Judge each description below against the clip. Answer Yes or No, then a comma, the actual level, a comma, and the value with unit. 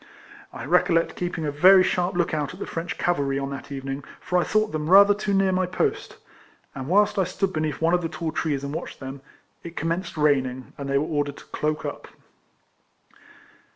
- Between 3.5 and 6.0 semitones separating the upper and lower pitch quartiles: Yes, average, 4.3 semitones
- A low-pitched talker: No, medium, 165 Hz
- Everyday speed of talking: No, fast, 210 wpm